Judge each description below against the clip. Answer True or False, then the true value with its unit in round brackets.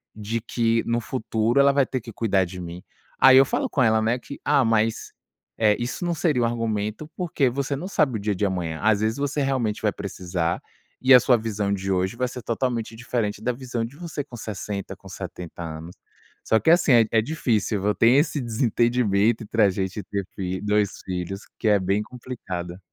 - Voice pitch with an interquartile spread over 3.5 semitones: True (4.0 semitones)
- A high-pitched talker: False (110 Hz)